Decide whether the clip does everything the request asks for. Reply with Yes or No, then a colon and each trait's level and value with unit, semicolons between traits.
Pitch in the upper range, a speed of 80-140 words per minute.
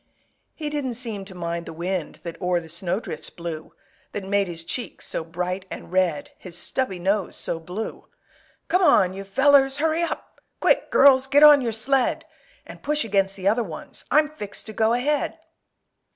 No: high, 200 Hz; average, 180 wpm